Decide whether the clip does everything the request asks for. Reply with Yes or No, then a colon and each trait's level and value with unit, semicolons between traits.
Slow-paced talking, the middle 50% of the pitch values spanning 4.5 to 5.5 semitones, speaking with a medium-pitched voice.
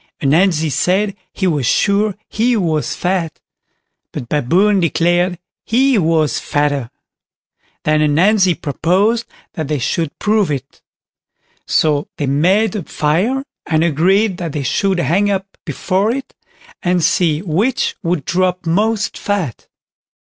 Yes: slow, 130 wpm; average, 4.8 semitones; medium, 175 Hz